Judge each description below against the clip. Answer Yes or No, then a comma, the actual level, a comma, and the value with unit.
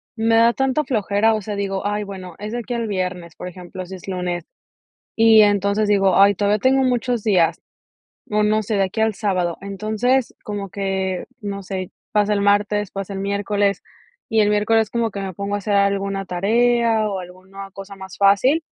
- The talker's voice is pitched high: Yes, high, 200 Hz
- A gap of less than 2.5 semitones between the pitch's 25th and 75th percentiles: Yes, narrow, 2.1 semitones